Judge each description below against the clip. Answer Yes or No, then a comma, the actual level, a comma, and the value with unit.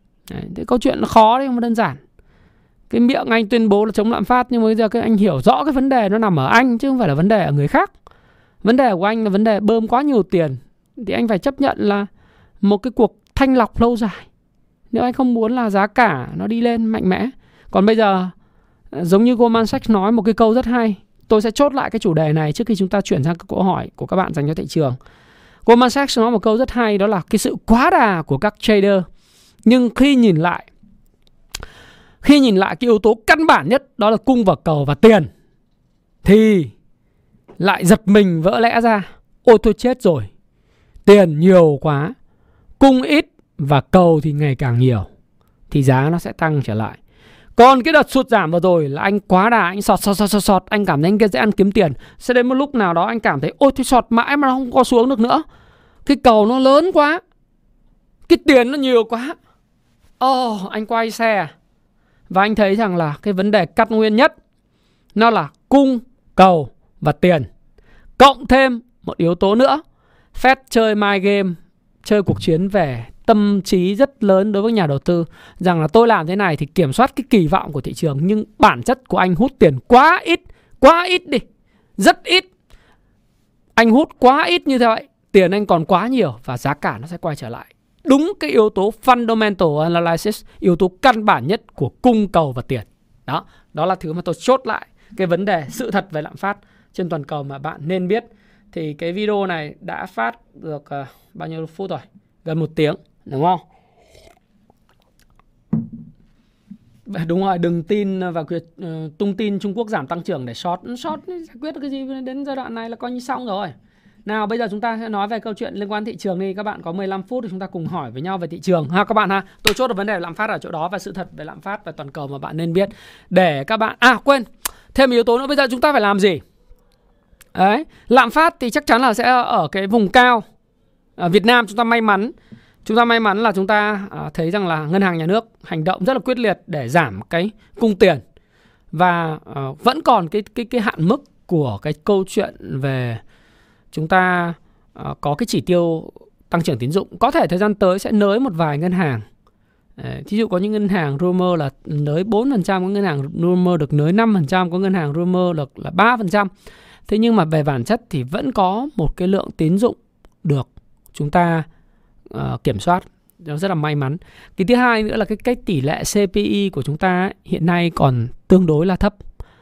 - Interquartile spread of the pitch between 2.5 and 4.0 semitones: No, wide, 5.4 semitones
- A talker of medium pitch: No, high, 200 Hz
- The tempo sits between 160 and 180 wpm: No, average, 225 wpm